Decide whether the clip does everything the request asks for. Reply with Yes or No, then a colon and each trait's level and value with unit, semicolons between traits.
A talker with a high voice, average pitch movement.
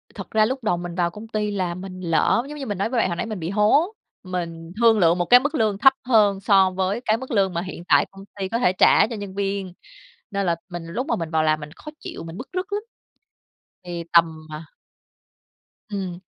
Yes: high, 195 Hz; average, 4.3 semitones